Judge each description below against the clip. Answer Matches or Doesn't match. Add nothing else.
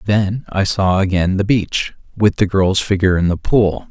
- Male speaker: Matches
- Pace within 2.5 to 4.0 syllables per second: Doesn't match